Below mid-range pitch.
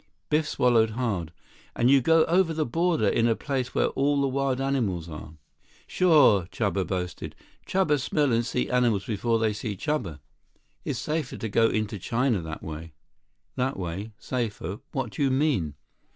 Yes: low, 120 Hz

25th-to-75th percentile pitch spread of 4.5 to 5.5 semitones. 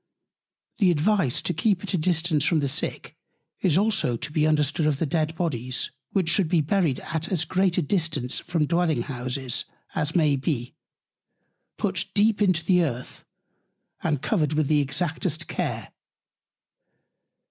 No: average, 3.8 semitones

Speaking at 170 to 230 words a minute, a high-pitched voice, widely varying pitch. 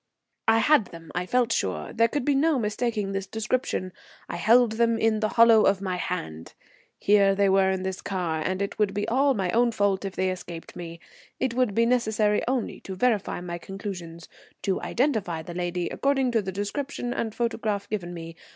No: average, 195 wpm; high, 205 Hz; average, 4.0 semitones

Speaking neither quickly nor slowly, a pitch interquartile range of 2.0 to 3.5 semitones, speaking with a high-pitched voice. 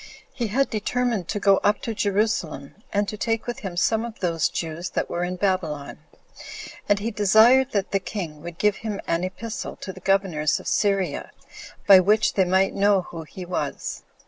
Yes: average, 190 wpm; average, 3.2 semitones; high, 195 Hz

